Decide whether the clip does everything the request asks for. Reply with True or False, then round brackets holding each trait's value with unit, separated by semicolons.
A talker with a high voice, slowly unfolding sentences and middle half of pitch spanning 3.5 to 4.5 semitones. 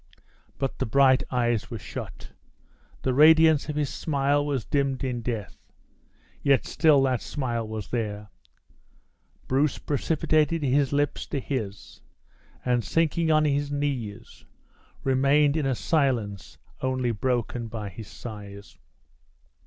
False (130 Hz; 125 wpm; 3.9 semitones)